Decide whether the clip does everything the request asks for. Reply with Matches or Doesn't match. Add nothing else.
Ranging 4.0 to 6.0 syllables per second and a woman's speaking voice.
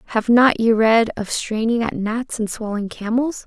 Matches